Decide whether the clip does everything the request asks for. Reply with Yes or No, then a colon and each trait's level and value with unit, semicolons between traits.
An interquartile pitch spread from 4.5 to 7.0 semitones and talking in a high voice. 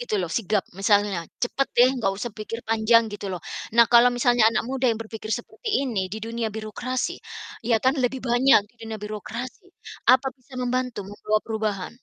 No: average, 2.8 semitones; high, 230 Hz